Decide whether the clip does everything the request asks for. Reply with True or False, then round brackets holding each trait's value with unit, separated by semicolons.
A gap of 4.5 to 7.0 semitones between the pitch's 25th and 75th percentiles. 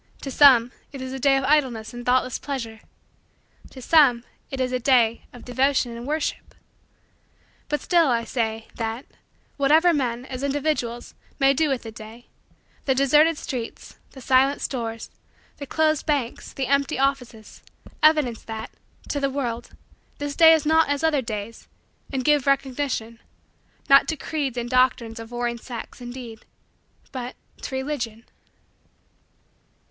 False (3.2 semitones)